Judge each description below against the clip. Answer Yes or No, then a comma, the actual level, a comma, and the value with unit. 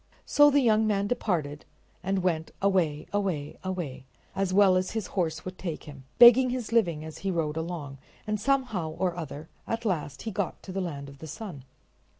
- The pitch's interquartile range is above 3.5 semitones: Yes, average, 5.0 semitones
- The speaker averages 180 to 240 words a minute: Yes, average, 190 wpm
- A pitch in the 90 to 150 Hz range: No, medium, 185 Hz